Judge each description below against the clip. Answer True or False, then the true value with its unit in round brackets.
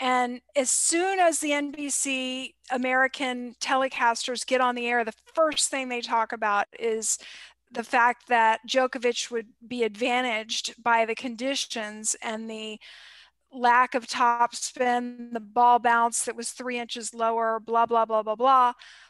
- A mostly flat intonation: True (2.0 semitones)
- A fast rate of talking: False (150 wpm)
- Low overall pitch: False (240 Hz)